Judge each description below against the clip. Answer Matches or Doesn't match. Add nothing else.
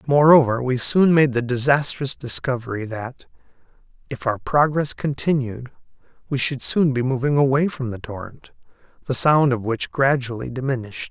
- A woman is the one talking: Doesn't match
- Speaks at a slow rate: Doesn't match